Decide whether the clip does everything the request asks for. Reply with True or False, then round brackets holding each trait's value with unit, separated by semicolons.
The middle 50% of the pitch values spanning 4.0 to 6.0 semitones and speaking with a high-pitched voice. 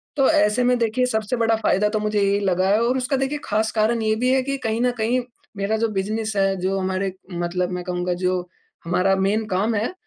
False (3.2 semitones; 215 Hz)